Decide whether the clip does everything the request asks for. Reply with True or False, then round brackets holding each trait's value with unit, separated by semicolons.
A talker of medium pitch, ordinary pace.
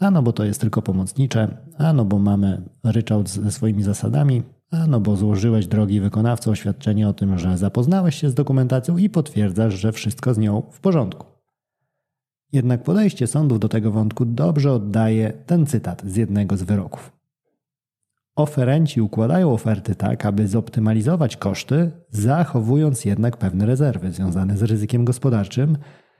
False (115 Hz; 150 wpm)